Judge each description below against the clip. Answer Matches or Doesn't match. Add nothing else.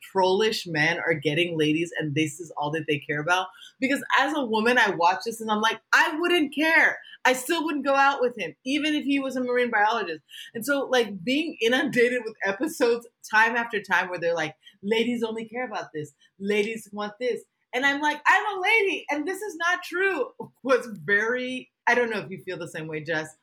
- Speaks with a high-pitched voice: Matches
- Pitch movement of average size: Doesn't match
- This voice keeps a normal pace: Doesn't match